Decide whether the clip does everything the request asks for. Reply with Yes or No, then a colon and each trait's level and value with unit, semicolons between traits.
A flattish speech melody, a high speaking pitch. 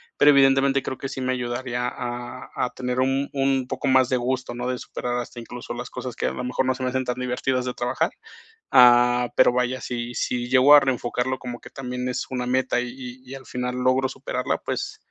No: narrow, 1.1 semitones; low, 125 Hz